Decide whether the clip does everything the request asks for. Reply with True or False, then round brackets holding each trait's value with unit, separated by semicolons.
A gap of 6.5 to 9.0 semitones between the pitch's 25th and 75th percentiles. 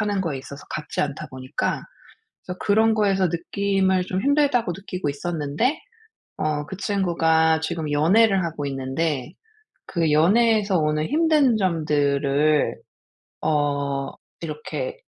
False (5.2 semitones)